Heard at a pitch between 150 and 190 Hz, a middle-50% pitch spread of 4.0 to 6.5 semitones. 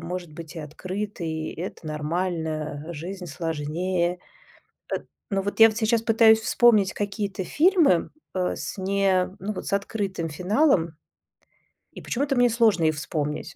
Yes: medium, 185 Hz; average, 4.5 semitones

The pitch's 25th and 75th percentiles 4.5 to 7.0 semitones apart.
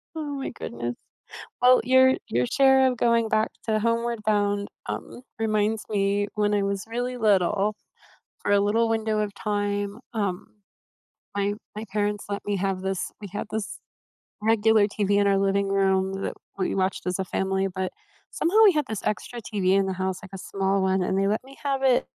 No: narrow, 2.4 semitones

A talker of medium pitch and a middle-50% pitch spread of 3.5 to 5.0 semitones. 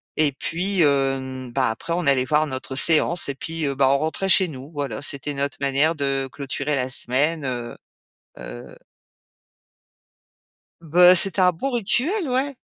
Yes: medium, 145 Hz; average, 4.1 semitones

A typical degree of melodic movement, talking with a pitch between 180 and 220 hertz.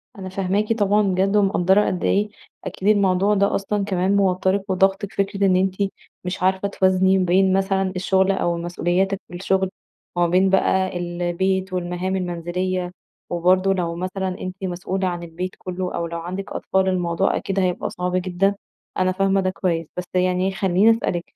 No: narrow, 1.3 semitones; medium, 185 Hz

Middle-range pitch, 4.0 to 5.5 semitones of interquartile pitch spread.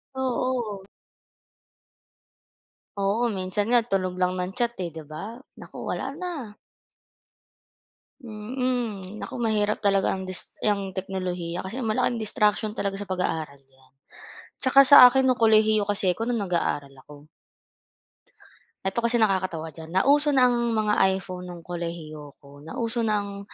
No: high, 205 Hz; average, 4.6 semitones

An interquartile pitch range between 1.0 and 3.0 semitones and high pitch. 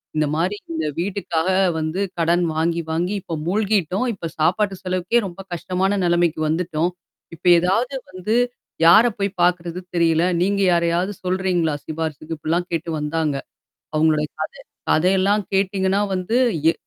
No: average, 2.7 semitones; medium, 175 Hz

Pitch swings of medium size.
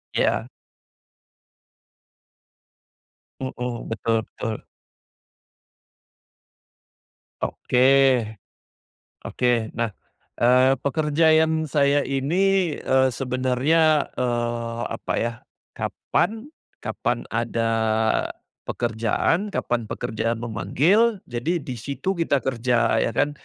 Yes: average, 4.5 semitones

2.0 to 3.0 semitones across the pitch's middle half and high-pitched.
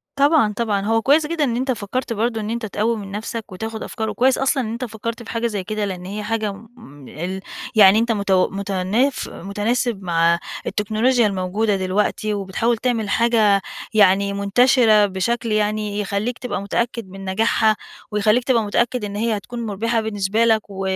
Yes: average, 2.7 semitones; high, 215 Hz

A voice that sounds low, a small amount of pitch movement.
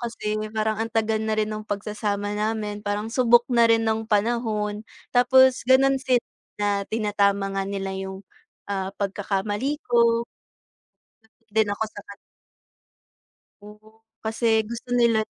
No: high, 215 Hz; narrow, 2.1 semitones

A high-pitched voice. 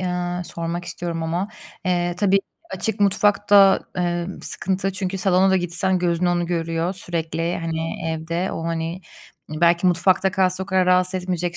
No: medium, 180 Hz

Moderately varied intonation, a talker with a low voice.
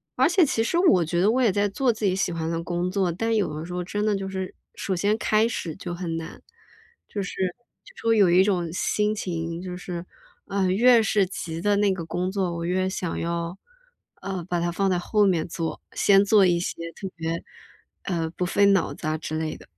No: average, 3.1 semitones; medium, 185 Hz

